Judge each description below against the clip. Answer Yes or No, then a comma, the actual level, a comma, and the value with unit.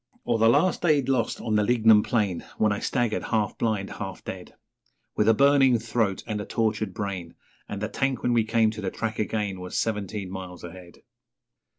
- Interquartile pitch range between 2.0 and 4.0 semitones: Yes, average, 2.8 semitones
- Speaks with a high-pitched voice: No, low, 110 Hz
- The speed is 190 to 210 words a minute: Yes, average, 195 wpm